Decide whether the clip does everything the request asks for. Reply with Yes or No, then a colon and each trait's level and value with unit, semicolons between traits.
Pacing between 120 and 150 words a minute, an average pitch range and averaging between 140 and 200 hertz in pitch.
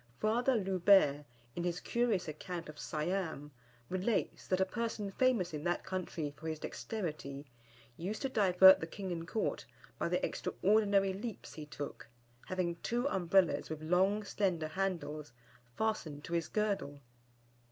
Yes: average, 145 wpm; average, 4.3 semitones; medium, 185 Hz